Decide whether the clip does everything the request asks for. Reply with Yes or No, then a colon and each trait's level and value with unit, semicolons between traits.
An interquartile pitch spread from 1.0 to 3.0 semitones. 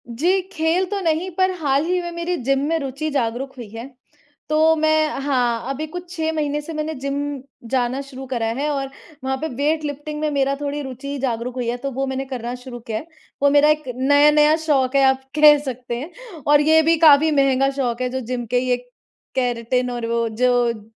No: average, 3.4 semitones